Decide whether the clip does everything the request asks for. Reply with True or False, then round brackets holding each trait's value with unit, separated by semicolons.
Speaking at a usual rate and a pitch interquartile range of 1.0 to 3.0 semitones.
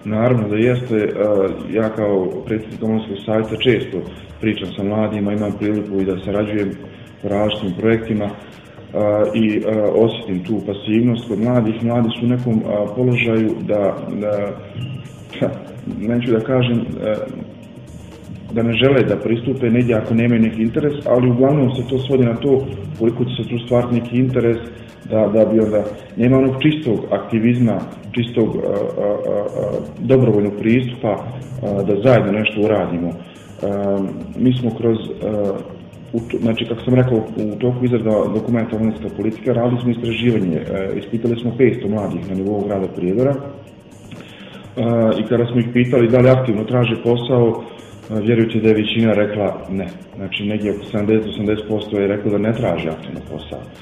True (150 wpm; 2.7 semitones)